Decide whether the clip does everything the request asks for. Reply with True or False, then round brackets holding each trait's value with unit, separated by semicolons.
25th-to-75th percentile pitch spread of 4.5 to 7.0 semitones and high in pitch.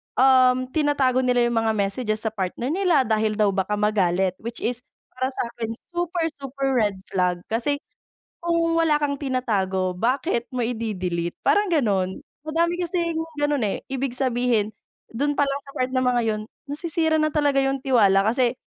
True (5.1 semitones; 250 Hz)